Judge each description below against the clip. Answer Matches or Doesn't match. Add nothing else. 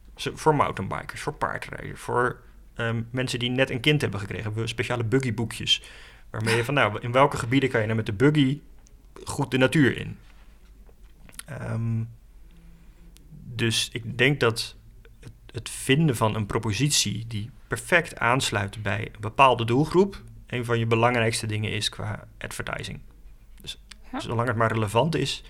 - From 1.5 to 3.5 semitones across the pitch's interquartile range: Matches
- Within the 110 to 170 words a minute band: Matches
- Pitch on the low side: Matches